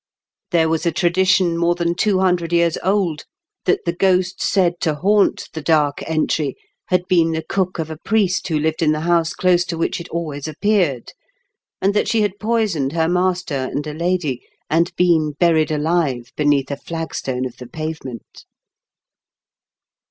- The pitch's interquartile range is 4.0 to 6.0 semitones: No, average, 2.9 semitones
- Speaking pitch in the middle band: Yes, medium, 170 Hz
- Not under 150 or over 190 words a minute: Yes, average, 170 wpm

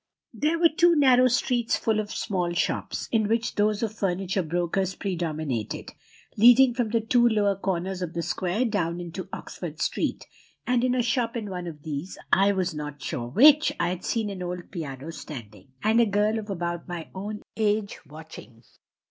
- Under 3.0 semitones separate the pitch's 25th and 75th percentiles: No, average, 4.8 semitones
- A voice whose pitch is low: No, high, 195 Hz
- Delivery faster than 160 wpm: Yes, average, 180 wpm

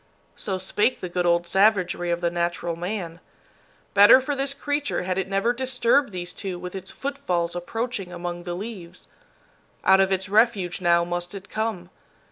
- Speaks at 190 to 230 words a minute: No, average, 170 wpm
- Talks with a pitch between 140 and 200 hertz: Yes, medium, 185 Hz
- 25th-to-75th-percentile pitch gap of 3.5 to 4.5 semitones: Yes, average, 4.0 semitones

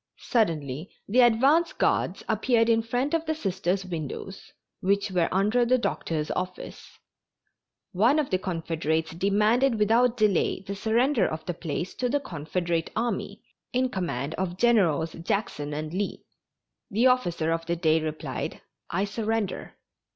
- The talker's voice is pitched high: Yes, high, 195 Hz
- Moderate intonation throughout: No, wide, 6.1 semitones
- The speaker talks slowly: No, average, 145 wpm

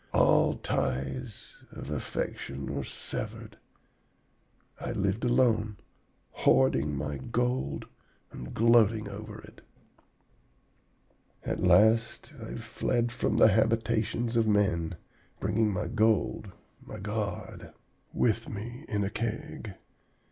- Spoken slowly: Yes, slow, 105 wpm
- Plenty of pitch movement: No, average, 3.9 semitones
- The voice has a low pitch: Yes, low, 110 Hz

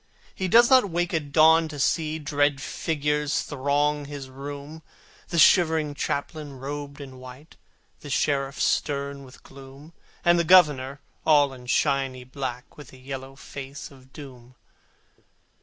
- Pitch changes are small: Yes, narrow, 2.3 semitones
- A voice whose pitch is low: No, medium, 145 Hz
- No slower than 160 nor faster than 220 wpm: No, average, 140 wpm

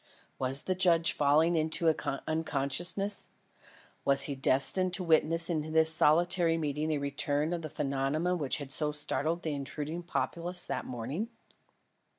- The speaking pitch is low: No, medium, 155 Hz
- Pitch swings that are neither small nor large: Yes, average, 3.1 semitones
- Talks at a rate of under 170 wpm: Yes, average, 150 wpm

